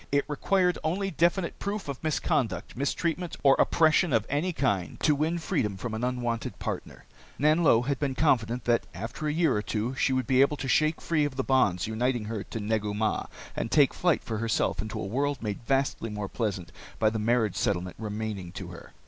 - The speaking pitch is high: No, low, 125 Hz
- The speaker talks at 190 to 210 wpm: Yes, average, 200 wpm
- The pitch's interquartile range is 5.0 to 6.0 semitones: Yes, wide, 5.6 semitones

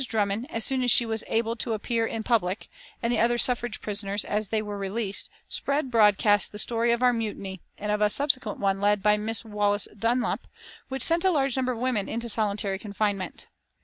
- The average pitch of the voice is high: Yes, high, 220 Hz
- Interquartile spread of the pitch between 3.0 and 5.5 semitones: No, narrow, 2.6 semitones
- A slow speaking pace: No, fast, 205 wpm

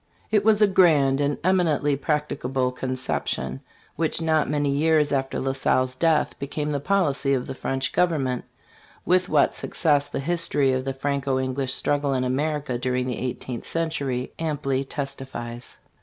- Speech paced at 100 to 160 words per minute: Yes, average, 155 wpm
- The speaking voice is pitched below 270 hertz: Yes, medium, 140 Hz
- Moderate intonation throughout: Yes, average, 3.0 semitones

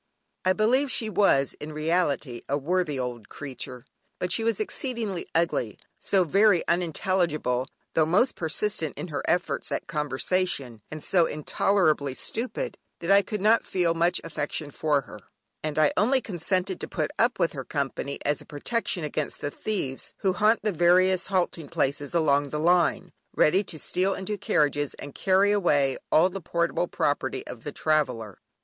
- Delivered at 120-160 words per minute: No, average, 170 wpm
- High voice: No, medium, 165 Hz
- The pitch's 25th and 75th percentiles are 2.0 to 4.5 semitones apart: No, average, 4.9 semitones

